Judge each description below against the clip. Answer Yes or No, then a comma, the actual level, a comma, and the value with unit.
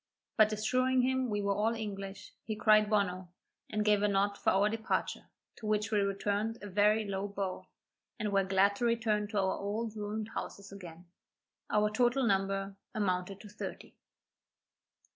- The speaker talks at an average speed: Yes, average, 165 wpm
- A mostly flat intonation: Yes, narrow, 1.6 semitones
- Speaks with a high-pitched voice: Yes, high, 210 Hz